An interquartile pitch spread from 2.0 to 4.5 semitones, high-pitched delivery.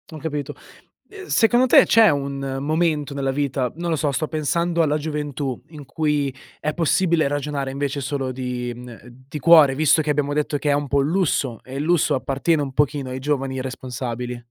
No: narrow, 2.6 semitones; medium, 145 Hz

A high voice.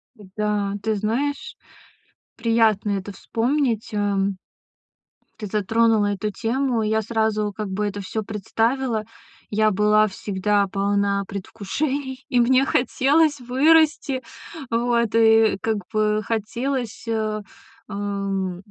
Yes: high, 220 Hz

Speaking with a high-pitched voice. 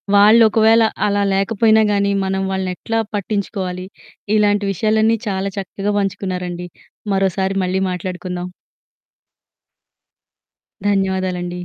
Yes: high, 195 Hz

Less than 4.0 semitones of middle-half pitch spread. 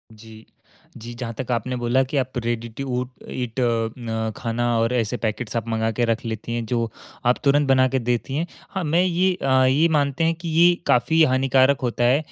Yes: average, 3.1 semitones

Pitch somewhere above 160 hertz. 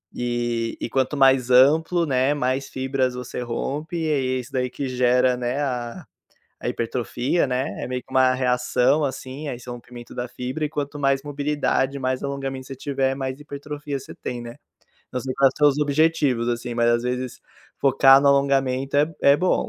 No: low, 130 Hz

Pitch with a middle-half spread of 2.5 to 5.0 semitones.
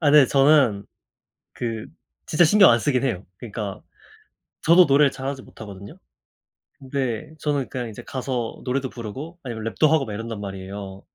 Yes: average, 4.7 semitones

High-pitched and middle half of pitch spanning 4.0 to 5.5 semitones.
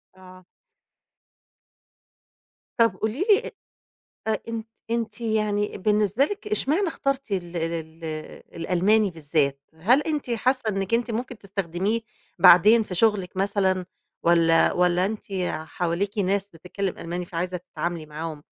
Yes: high, 195 Hz; average, 4.4 semitones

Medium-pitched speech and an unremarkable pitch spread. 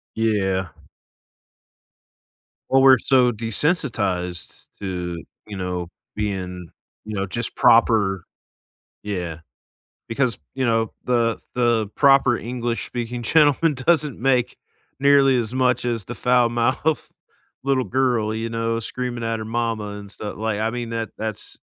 No: low, 115 Hz; average, 3.3 semitones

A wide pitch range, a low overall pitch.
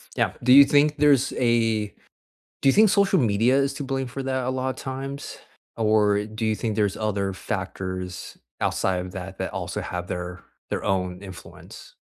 Yes: wide, 5.7 semitones; low, 110 Hz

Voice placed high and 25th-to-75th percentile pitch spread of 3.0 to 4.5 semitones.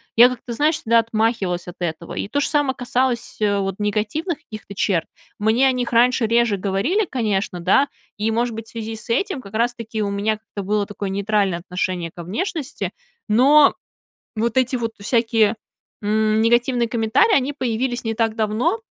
Yes: high, 225 Hz; average, 3.3 semitones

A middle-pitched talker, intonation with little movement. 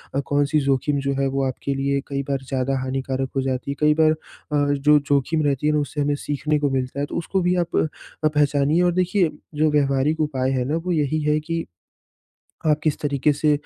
Yes: medium, 145 Hz; narrow, 1.8 semitones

